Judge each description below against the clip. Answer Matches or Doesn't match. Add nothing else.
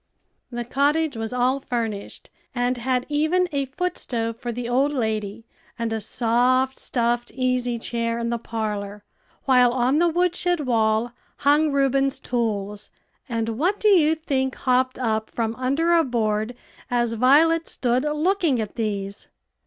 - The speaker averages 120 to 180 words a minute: Matches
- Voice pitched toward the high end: Matches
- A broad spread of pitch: Doesn't match